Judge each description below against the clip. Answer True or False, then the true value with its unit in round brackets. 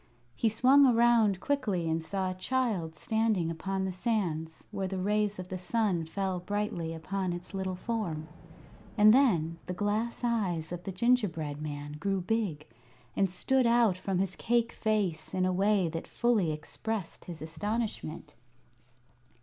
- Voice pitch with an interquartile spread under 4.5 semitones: False (4.8 semitones)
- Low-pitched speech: False (190 Hz)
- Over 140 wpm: True (155 wpm)